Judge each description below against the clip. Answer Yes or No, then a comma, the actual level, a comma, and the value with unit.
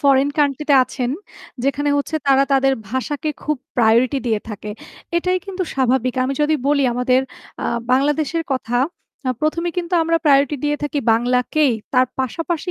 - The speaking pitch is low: No, very high, 275 Hz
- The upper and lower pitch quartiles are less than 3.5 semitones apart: Yes, average, 3.1 semitones